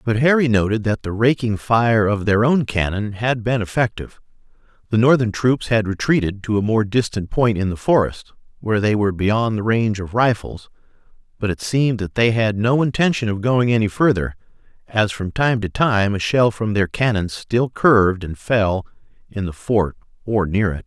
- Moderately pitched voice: No, low, 110 Hz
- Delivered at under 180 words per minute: No, average, 195 wpm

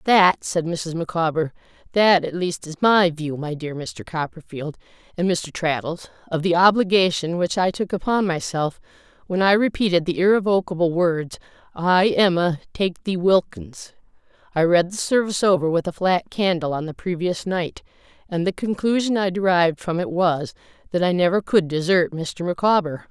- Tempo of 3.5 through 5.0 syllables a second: Yes, 4.9 syllables/s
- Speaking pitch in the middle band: Yes, medium, 175 Hz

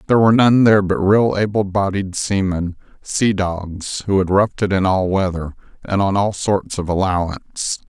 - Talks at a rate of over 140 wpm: Yes, average, 175 wpm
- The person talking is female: No, male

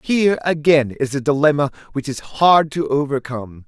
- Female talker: No, male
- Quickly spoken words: No, average, 165 wpm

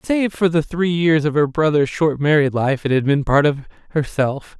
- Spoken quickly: Yes, fast, 220 wpm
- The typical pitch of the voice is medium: Yes, medium, 150 Hz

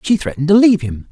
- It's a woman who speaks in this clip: Yes, female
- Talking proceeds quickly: Yes, fast, 270 wpm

